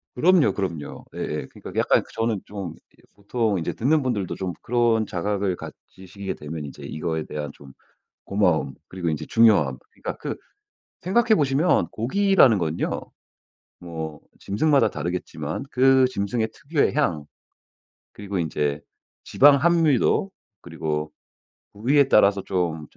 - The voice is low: Yes, low, 100 Hz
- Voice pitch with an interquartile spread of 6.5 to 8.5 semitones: Yes, wide, 8.0 semitones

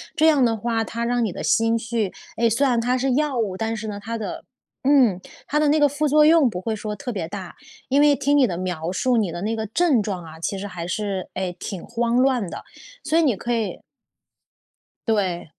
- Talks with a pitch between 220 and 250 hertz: Yes, high, 225 Hz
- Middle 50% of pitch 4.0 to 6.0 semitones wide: Yes, average, 5.0 semitones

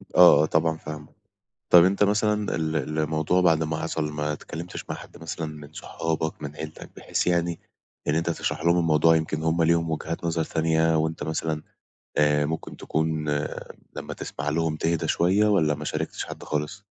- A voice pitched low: Yes, very low, 80 Hz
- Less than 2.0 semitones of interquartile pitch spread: Yes, narrow, 1.5 semitones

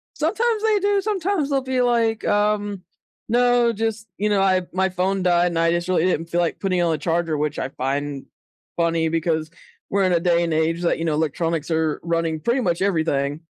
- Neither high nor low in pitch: Yes, medium, 180 Hz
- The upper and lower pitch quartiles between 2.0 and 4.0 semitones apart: No, wide, 5.4 semitones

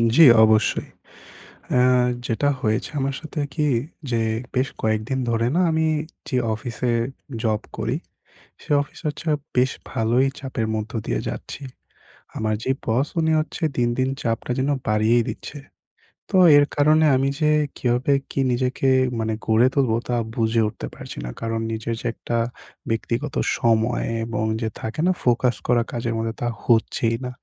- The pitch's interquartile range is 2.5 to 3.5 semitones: Yes, average, 3.1 semitones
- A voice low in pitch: Yes, low, 120 Hz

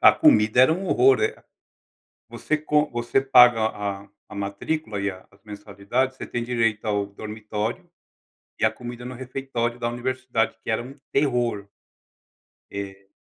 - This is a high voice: No, low, 120 Hz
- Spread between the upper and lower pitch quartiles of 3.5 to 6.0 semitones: Yes, average, 3.9 semitones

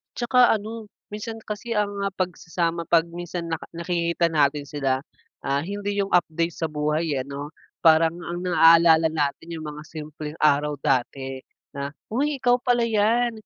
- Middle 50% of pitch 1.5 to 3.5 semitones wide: No, average, 5.3 semitones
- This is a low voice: No, medium, 170 Hz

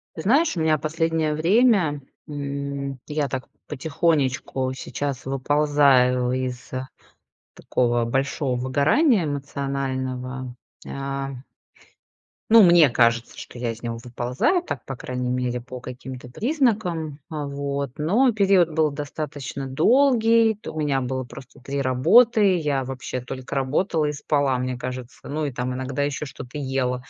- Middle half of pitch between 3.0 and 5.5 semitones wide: Yes, average, 3.7 semitones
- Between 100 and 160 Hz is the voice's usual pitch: Yes, medium, 140 Hz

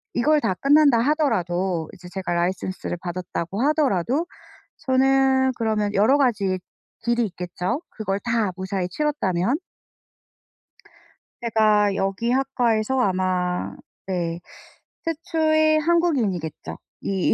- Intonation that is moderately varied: No, wide, 6.4 semitones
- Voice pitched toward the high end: Yes, high, 215 Hz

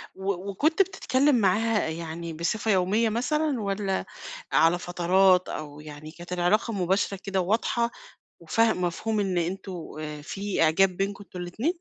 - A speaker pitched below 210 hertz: Yes, high, 190 Hz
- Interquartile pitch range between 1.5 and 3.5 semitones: No, average, 4.0 semitones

